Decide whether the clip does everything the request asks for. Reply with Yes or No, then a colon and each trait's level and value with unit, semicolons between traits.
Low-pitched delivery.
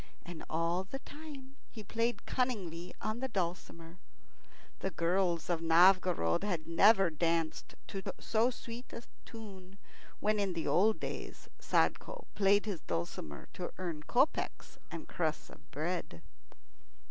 No: medium, 185 Hz